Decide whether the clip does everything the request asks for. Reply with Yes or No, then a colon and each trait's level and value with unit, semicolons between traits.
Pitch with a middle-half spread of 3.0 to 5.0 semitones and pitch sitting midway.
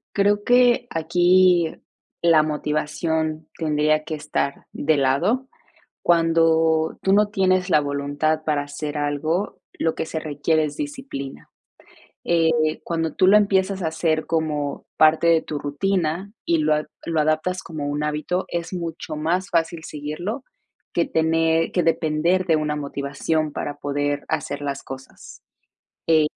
No: narrow, 2.4 semitones; medium, 160 Hz